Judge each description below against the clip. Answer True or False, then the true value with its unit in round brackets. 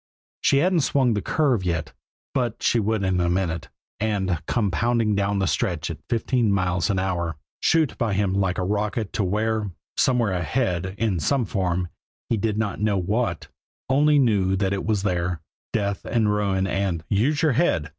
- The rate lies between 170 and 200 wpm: True (180 wpm)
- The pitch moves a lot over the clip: False (3.8 semitones)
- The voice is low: True (100 Hz)